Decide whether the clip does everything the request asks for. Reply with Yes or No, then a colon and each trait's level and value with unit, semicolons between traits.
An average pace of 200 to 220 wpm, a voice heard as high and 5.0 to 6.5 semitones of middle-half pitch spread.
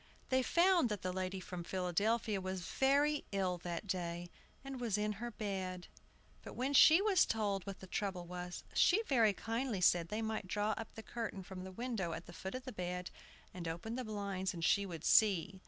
No: fast, 205 wpm; high, 200 Hz; average, 4.1 semitones